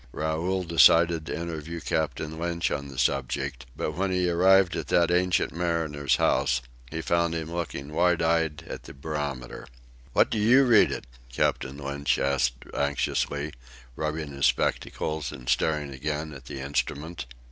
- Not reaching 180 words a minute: Yes, average, 155 wpm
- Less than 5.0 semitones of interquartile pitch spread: Yes, average, 3.2 semitones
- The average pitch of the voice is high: No, very low, 80 Hz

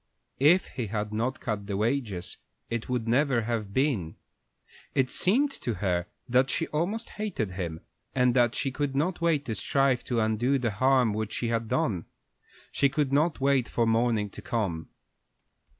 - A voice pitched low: Yes, low, 120 Hz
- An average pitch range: Yes, average, 4.4 semitones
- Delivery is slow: No, average, 170 wpm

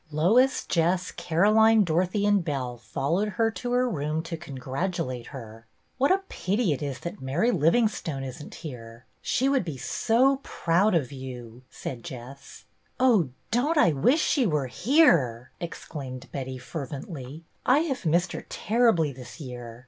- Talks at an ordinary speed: Yes, average, 170 wpm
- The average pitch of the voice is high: No, medium, 165 Hz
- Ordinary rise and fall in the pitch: No, wide, 8.7 semitones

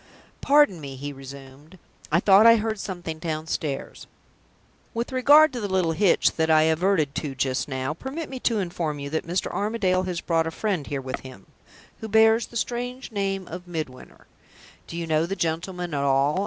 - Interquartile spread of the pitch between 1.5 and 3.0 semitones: No, wide, 5.6 semitones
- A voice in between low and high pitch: Yes, medium, 170 Hz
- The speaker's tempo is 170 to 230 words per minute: Yes, average, 185 wpm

